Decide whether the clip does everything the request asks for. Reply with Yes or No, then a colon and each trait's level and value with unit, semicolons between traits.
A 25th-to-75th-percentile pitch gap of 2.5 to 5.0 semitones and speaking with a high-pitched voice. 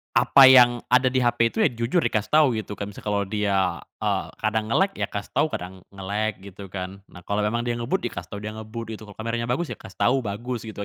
No: average, 3.0 semitones; low, 110 Hz